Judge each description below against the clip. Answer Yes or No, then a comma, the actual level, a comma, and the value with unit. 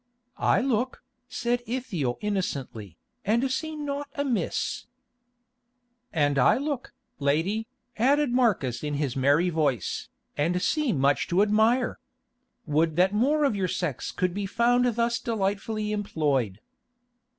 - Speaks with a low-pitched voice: No, high, 205 Hz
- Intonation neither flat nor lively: No, wide, 8.5 semitones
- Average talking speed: No, slow, 125 wpm